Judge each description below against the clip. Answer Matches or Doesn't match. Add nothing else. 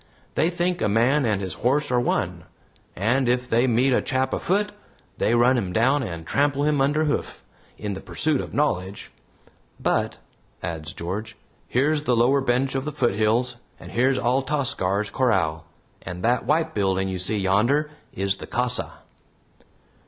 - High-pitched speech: Doesn't match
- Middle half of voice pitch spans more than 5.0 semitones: Matches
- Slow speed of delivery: Doesn't match